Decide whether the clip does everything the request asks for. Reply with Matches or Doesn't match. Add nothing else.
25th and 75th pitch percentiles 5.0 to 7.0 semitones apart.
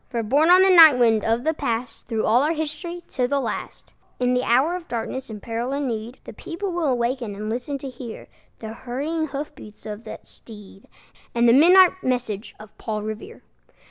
Matches